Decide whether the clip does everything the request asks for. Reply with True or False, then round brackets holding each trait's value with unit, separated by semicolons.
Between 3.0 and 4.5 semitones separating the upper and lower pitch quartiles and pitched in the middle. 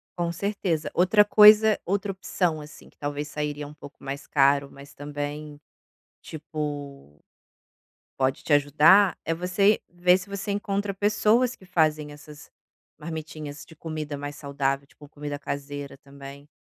True (4.2 semitones; 150 Hz)